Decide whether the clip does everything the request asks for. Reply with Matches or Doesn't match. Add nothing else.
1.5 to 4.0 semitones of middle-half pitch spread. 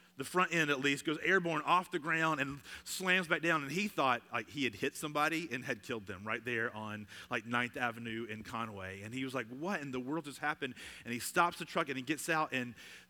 Doesn't match